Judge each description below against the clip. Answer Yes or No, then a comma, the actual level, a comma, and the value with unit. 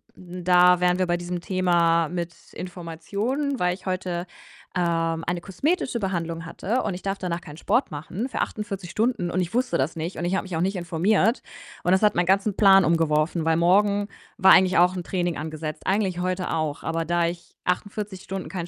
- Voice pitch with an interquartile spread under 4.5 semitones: Yes, narrow, 2.4 semitones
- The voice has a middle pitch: Yes, medium, 180 Hz